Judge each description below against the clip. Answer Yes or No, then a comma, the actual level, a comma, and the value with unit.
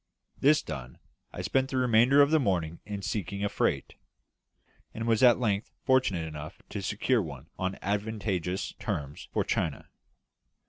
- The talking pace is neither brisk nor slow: Yes, average, 150 wpm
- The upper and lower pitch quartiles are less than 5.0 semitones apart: No, wide, 5.6 semitones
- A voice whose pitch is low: Yes, low, 105 Hz